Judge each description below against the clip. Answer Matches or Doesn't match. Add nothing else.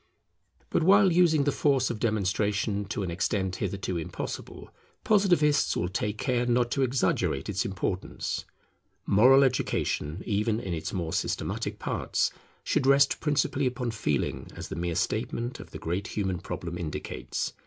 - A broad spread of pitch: Matches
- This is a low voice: Matches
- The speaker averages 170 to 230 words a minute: Doesn't match